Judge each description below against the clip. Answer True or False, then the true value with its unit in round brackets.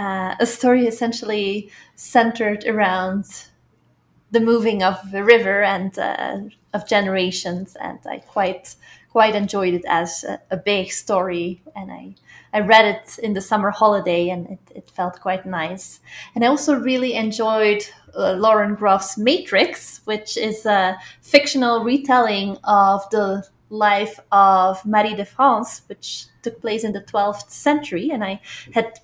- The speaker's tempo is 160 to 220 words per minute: False (150 wpm)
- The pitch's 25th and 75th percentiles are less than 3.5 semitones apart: True (2.7 semitones)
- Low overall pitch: False (210 Hz)